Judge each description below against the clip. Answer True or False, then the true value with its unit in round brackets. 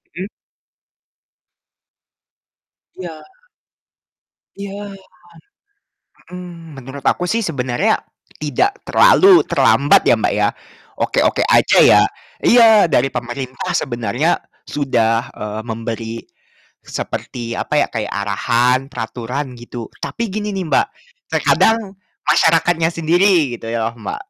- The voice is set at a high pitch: False (140 Hz)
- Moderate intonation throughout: False (7.5 semitones)